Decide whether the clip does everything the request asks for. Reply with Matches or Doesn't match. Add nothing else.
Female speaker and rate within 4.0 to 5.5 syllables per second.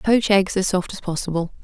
Matches